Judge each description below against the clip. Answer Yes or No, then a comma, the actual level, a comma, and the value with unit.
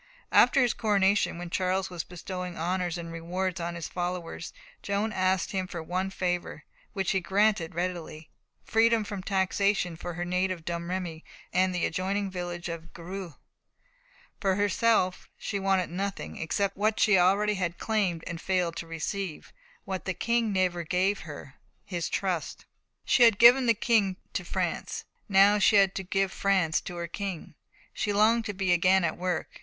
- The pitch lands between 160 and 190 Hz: Yes, medium, 185 Hz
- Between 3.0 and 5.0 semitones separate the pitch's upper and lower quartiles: No, narrow, 2.4 semitones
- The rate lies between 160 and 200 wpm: Yes, average, 165 wpm